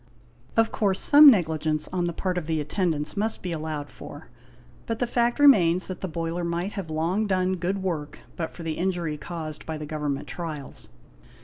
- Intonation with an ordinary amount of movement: Yes, average, 3.4 semitones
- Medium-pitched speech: Yes, medium, 170 Hz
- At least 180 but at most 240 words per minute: Yes, average, 195 wpm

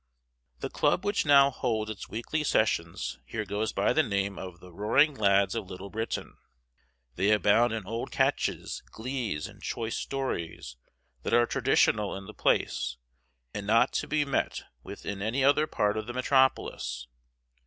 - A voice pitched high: No, low, 110 Hz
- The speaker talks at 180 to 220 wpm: No, average, 165 wpm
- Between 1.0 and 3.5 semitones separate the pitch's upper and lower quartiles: No, average, 4.8 semitones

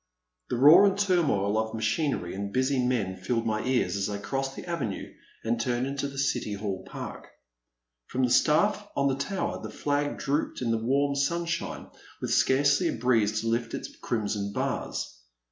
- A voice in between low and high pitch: No, low, 125 Hz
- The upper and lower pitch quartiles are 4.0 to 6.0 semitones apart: Yes, average, 4.8 semitones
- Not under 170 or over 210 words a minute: Yes, average, 180 wpm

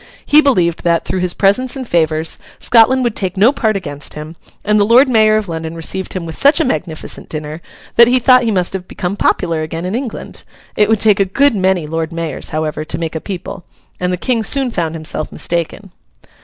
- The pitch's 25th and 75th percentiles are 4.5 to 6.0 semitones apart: Yes, wide, 5.4 semitones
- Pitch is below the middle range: No, medium, 185 Hz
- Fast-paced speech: Yes, fast, 215 wpm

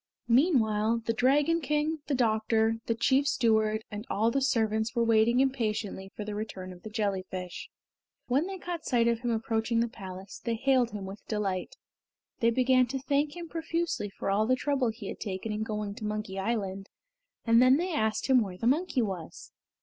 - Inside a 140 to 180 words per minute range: No, average, 190 wpm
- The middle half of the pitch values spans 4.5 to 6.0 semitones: No, average, 3.8 semitones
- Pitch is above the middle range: Yes, high, 225 Hz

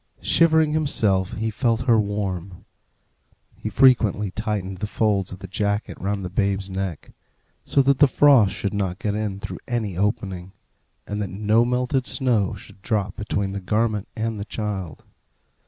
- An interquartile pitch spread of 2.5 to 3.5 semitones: Yes, average, 2.8 semitones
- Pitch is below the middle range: Yes, low, 105 Hz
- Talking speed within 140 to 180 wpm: Yes, average, 160 wpm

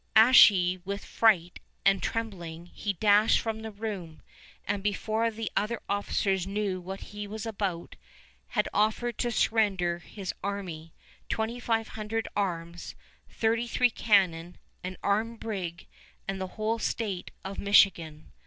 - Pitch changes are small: No, average, 3.3 semitones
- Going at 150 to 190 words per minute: No, slow, 135 wpm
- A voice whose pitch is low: No, high, 200 Hz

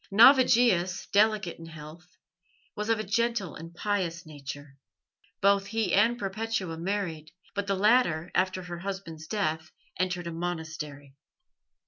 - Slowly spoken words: Yes, slow, 130 wpm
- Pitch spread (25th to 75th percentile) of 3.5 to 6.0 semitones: Yes, average, 4.2 semitones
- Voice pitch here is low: No, medium, 185 Hz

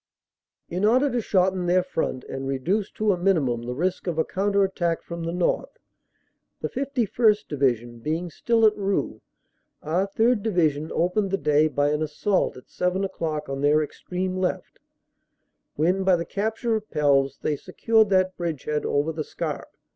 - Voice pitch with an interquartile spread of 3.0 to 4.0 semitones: No, average, 4.8 semitones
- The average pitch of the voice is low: No, medium, 180 Hz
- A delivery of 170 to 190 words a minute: Yes, average, 175 wpm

